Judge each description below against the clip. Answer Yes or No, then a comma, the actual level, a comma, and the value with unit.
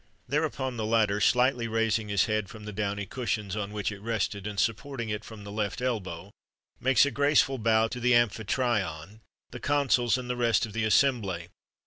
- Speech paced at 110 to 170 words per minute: No, average, 190 wpm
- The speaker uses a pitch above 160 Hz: No, low, 110 Hz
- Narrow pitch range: No, average, 3.2 semitones